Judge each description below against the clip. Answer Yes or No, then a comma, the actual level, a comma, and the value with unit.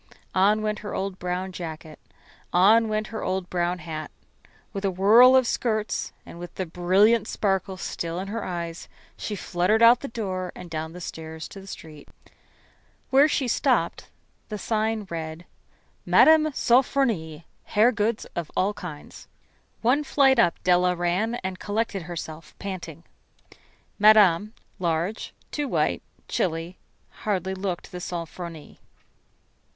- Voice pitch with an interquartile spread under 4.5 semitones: Yes, average, 3.9 semitones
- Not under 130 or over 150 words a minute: Yes, average, 140 wpm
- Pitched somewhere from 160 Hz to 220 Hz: Yes, high, 190 Hz